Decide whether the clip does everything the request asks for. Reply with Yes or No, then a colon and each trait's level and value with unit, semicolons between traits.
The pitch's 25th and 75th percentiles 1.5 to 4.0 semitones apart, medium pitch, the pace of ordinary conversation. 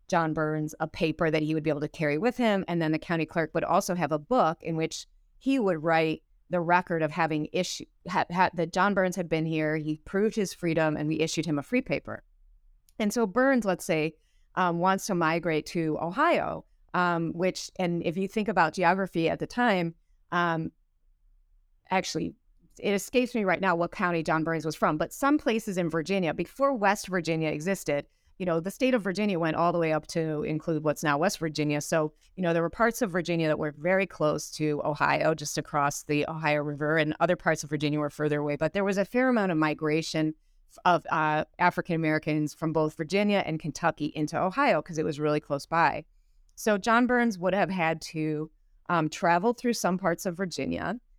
No: average, 3.4 semitones; medium, 165 Hz; fast, 210 wpm